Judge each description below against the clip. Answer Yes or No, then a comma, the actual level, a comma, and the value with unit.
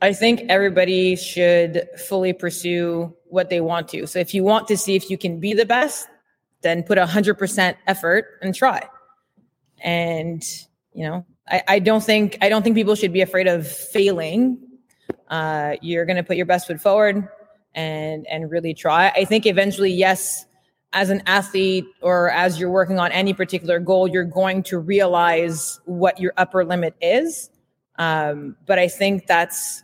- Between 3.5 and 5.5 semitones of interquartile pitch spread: No, narrow, 2.5 semitones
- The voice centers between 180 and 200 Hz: Yes, medium, 185 Hz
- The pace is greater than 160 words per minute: Yes, average, 175 wpm